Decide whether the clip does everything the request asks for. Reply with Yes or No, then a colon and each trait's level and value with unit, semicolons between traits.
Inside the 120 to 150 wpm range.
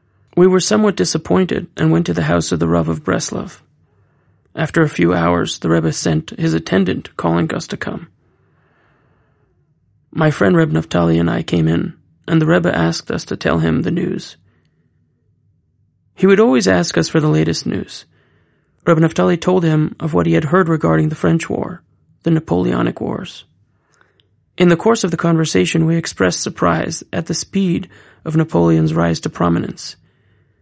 No: average, 170 wpm